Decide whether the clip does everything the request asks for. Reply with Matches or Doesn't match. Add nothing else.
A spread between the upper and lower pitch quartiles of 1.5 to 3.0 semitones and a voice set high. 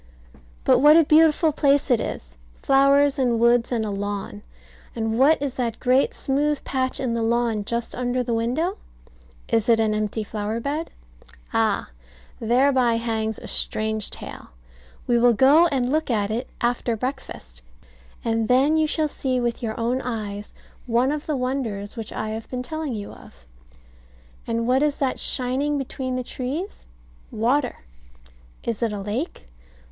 Doesn't match